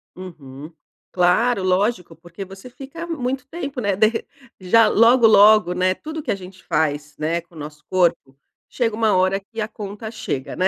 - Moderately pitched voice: No, high, 195 Hz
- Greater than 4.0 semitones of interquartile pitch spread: Yes, average, 4.8 semitones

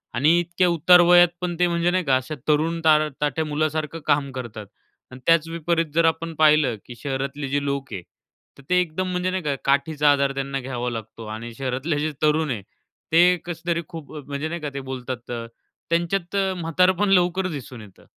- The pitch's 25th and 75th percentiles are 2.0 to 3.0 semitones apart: No, average, 3.8 semitones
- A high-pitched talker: No, medium, 155 Hz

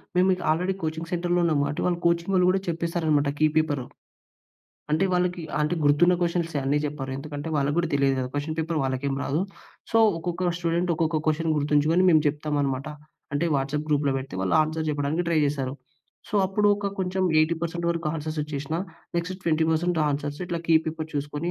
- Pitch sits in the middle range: Yes, medium, 160 Hz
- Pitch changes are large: No, average, 2.9 semitones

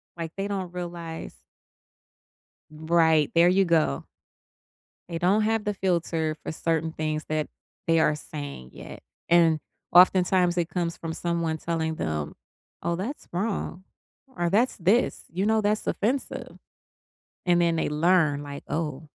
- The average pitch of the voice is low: No, medium, 170 Hz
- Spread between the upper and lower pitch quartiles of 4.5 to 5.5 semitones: No, average, 2.7 semitones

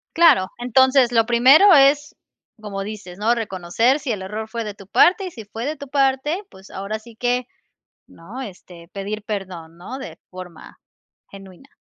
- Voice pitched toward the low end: No, high, 225 Hz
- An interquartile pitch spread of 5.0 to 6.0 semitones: Yes, average, 5.3 semitones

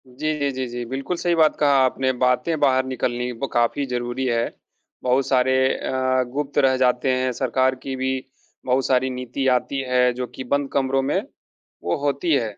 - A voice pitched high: No, low, 130 Hz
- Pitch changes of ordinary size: No, narrow, 1.5 semitones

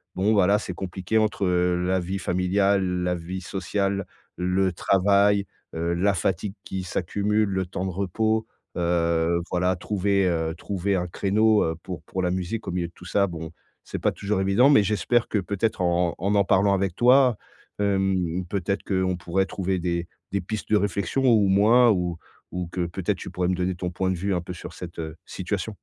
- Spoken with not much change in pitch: Yes, narrow, 2.3 semitones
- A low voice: Yes, very low, 95 Hz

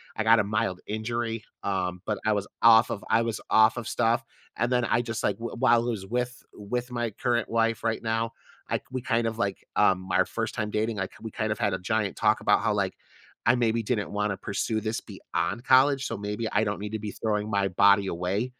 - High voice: No, low, 110 Hz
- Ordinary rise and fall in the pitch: No, narrow, 2.2 semitones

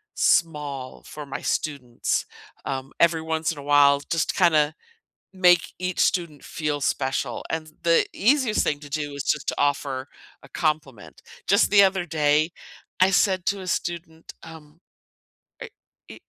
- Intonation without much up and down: No, average, 3.3 semitones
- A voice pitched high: No, medium, 155 Hz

